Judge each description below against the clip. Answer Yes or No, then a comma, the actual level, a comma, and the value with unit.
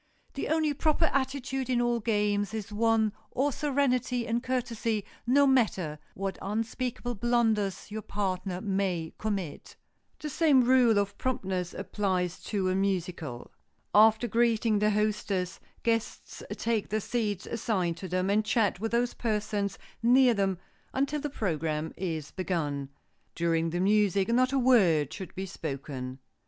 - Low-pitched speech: No, high, 210 Hz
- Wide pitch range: No, average, 4.5 semitones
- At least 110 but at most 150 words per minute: Yes, average, 145 wpm